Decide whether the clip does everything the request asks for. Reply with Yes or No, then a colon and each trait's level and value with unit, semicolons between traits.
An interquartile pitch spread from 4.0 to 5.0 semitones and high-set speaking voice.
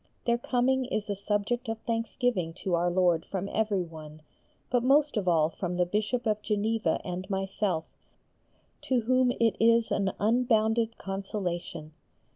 Yes: average, 4.5 semitones; high, 210 Hz